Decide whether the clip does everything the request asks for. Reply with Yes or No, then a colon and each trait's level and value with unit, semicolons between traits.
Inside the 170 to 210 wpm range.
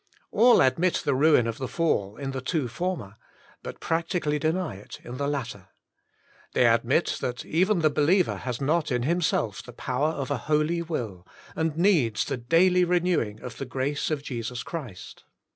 Yes: average, 175 wpm